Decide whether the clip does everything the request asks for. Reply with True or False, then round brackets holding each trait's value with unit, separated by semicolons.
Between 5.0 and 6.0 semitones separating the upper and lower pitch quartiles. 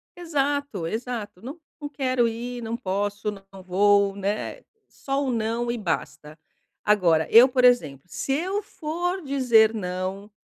True (5.5 semitones)